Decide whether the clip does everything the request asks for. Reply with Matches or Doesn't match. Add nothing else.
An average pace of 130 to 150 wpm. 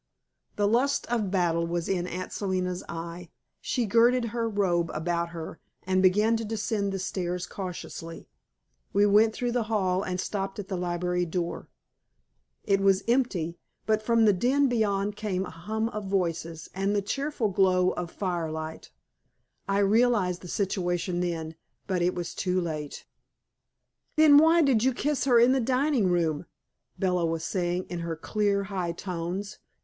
Doesn't match